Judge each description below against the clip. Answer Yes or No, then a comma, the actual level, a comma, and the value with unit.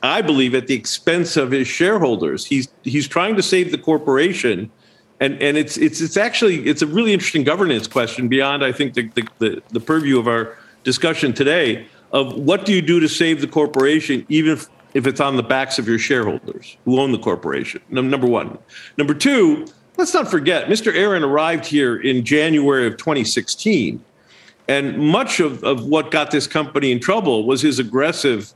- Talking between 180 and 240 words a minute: Yes, average, 185 wpm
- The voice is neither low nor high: Yes, medium, 145 Hz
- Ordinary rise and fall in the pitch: Yes, average, 3.4 semitones